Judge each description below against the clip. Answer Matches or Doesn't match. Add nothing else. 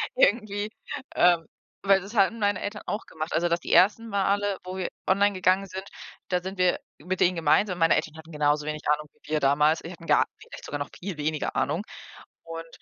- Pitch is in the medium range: Matches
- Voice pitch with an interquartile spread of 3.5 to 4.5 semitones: Matches